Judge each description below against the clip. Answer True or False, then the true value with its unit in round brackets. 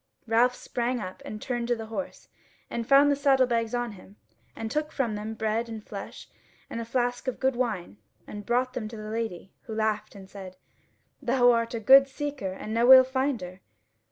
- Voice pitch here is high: True (235 Hz)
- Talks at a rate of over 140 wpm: True (200 wpm)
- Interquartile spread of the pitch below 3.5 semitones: True (3.0 semitones)